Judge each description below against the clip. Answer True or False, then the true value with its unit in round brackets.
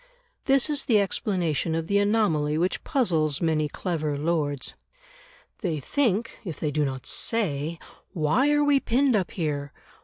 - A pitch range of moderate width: False (7.0 semitones)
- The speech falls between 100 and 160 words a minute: True (150 wpm)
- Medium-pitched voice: True (170 Hz)